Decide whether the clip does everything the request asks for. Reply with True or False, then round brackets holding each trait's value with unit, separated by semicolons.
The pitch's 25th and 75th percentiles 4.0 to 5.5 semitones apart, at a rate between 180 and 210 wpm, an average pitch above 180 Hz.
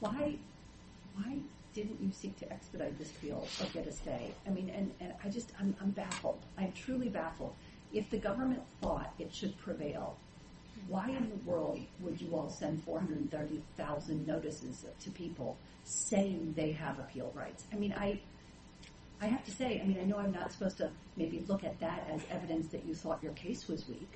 True (4.4 semitones; 190 wpm; 190 Hz)